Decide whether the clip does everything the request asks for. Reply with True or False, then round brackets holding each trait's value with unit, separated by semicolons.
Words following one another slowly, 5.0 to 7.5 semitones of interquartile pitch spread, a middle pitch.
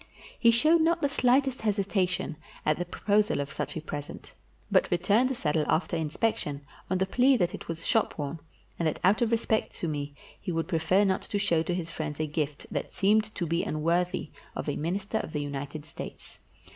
False (200 wpm; 5.6 semitones; 175 Hz)